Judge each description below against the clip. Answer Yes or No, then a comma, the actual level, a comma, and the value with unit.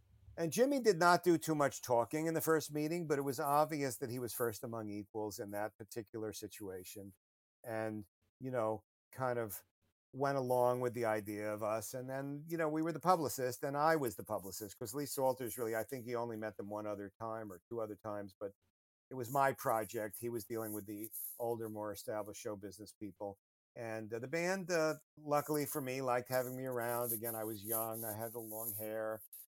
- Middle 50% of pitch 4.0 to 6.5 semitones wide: Yes, average, 4.5 semitones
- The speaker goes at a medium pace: No, fast, 215 wpm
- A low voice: Yes, low, 120 Hz